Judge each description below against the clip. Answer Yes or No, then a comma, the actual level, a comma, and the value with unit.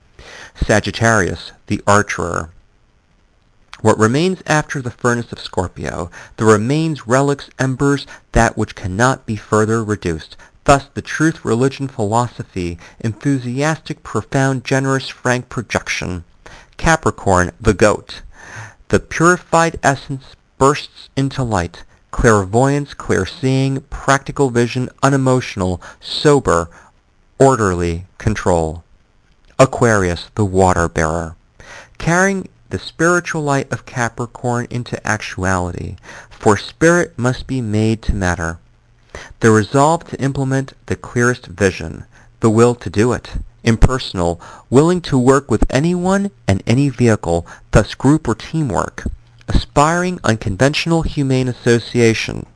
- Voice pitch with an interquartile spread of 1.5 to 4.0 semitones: No, average, 5.1 semitones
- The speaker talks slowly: Yes, slow, 110 wpm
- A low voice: Yes, low, 120 Hz